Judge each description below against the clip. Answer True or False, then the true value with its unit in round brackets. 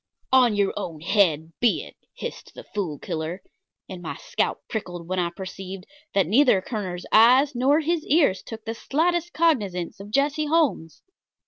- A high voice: True (205 Hz)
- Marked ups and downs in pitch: True (7.5 semitones)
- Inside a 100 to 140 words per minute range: False (160 wpm)